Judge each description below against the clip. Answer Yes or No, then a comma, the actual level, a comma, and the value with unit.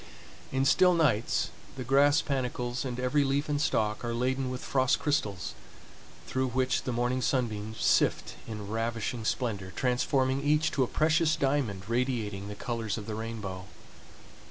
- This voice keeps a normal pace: Yes, average, 155 wpm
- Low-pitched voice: Yes, low, 125 Hz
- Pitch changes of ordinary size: Yes, average, 3.5 semitones